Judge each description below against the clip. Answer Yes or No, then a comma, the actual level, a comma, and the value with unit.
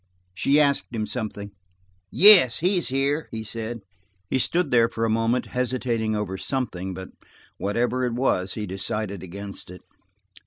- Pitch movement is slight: No, average, 4.1 semitones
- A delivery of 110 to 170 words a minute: Yes, average, 160 wpm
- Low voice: Yes, low, 115 Hz